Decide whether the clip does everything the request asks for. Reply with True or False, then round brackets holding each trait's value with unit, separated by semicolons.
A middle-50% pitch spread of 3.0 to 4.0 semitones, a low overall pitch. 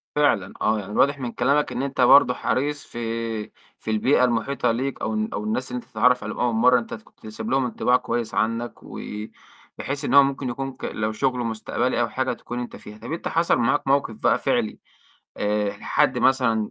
True (3.5 semitones; 125 Hz)